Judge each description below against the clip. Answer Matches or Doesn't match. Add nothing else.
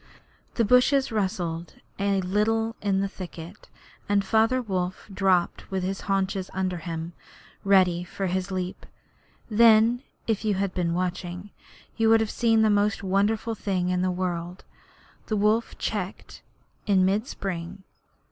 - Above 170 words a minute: Doesn't match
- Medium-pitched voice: Doesn't match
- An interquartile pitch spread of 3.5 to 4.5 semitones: Doesn't match